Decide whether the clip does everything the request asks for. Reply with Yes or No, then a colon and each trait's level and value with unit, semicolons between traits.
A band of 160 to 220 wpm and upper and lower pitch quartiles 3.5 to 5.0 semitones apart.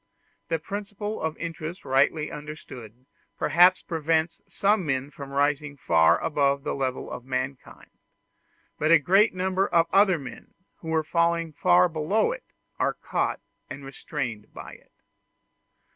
No: average, 140 wpm; average, 4.1 semitones